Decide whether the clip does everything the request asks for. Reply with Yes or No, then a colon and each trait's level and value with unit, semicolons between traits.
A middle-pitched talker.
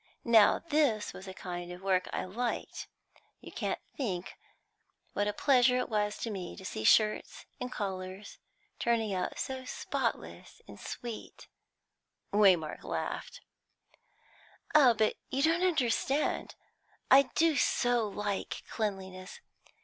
No: high, 215 Hz